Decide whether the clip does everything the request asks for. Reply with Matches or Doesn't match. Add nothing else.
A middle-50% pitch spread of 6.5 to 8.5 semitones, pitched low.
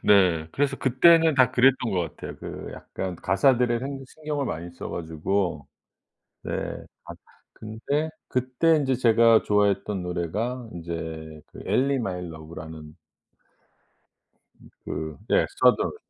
Matches